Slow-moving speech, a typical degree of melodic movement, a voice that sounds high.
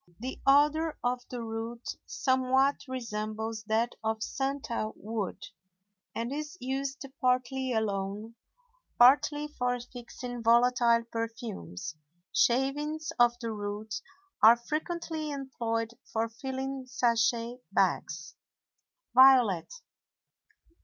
Yes: slow, 95 wpm; average, 3.1 semitones; high, 240 Hz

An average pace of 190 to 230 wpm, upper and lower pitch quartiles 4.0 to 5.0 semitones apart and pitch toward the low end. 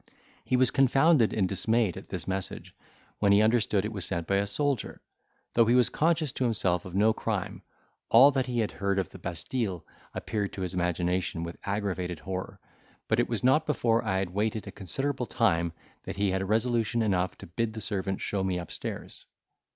Yes: average, 195 wpm; average, 4.3 semitones; low, 105 Hz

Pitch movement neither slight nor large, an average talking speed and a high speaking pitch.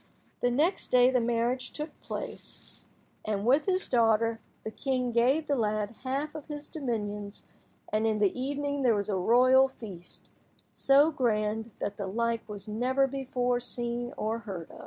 Yes: average, 3.8 semitones; average, 160 wpm; high, 240 Hz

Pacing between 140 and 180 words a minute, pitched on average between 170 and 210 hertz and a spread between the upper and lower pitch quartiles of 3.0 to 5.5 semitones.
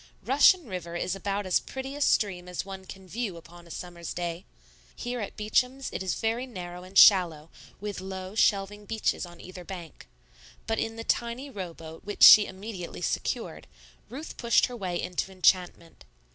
Yes: average, 175 wpm; high, 190 Hz; average, 4.0 semitones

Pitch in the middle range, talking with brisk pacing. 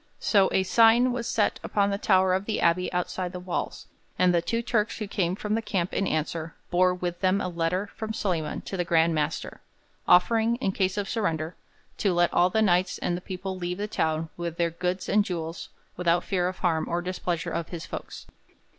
Yes: medium, 180 Hz; fast, 210 wpm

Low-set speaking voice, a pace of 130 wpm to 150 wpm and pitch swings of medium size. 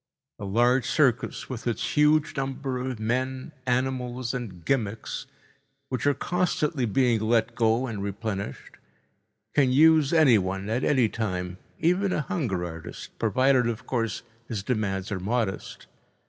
Yes: low, 120 Hz; slow, 135 wpm; average, 3.7 semitones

